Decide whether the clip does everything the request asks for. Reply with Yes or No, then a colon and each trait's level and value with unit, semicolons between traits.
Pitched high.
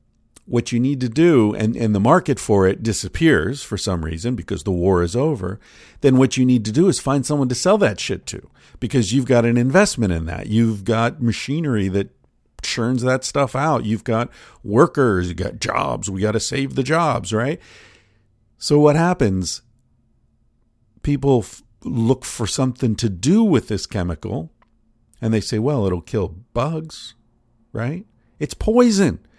No: low, 120 Hz